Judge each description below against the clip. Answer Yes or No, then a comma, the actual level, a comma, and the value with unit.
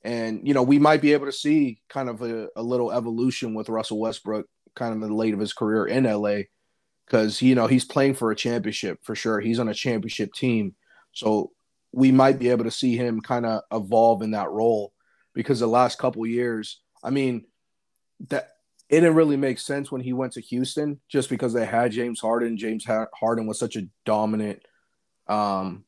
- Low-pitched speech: Yes, low, 115 Hz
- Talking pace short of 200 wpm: No, fast, 205 wpm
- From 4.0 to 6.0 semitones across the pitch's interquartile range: No, average, 2.8 semitones